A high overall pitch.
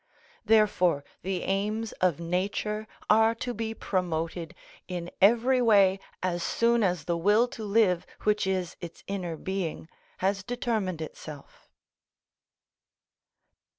Yes: high, 195 Hz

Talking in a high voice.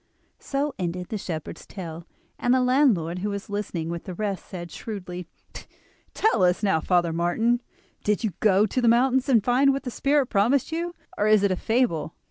Yes: high, 210 Hz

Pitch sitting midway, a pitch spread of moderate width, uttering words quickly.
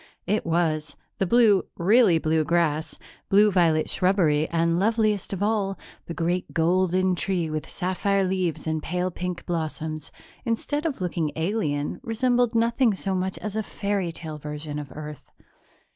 No: medium, 180 Hz; average, 4.2 semitones; average, 150 wpm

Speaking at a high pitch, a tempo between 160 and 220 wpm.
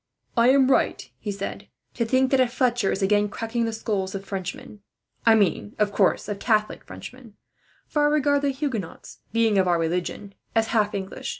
Yes: high, 220 Hz; average, 195 wpm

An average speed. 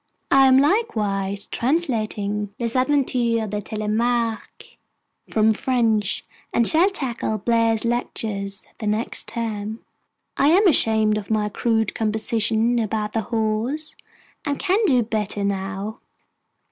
No: slow, 120 wpm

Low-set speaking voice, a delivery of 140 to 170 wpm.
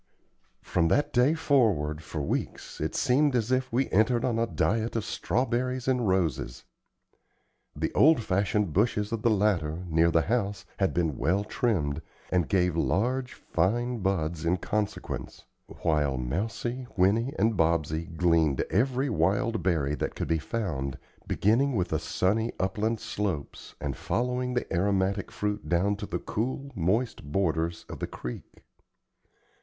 Yes: low, 100 Hz; average, 150 wpm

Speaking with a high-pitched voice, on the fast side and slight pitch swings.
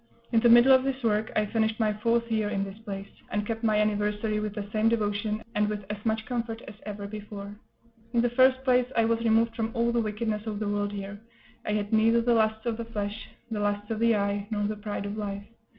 Yes: high, 215 Hz; fast, 240 wpm; narrow, 1.9 semitones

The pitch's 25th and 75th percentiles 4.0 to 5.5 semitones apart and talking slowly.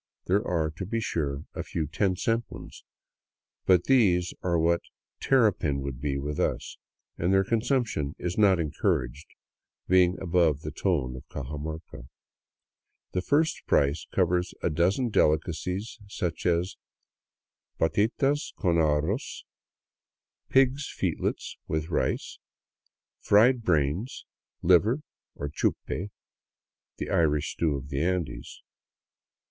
Yes: average, 5.2 semitones; slow, 125 wpm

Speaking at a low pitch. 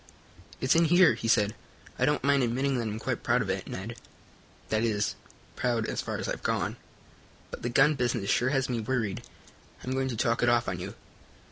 Yes: low, 120 Hz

